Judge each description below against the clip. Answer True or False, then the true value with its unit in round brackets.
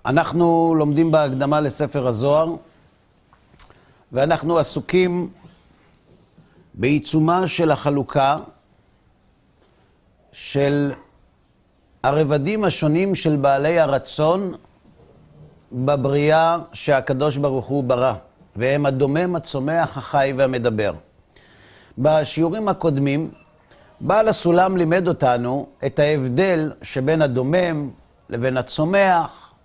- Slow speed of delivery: True (75 wpm)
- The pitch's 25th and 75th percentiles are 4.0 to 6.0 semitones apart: False (3.4 semitones)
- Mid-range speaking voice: True (150 Hz)